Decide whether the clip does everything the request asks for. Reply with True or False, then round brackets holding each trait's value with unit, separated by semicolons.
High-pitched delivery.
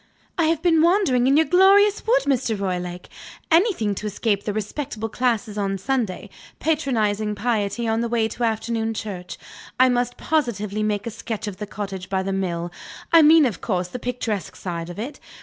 True (225 Hz)